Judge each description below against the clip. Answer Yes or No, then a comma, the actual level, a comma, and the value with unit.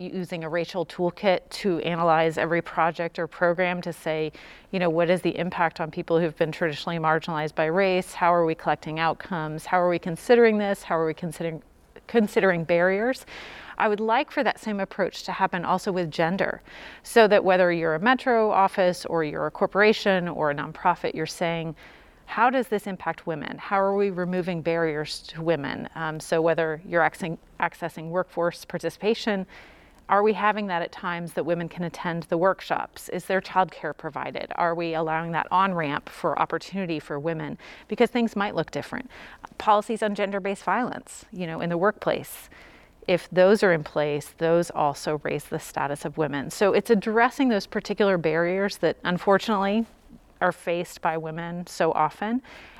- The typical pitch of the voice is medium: Yes, medium, 175 Hz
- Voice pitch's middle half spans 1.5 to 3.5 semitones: Yes, average, 3.1 semitones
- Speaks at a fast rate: No, average, 175 wpm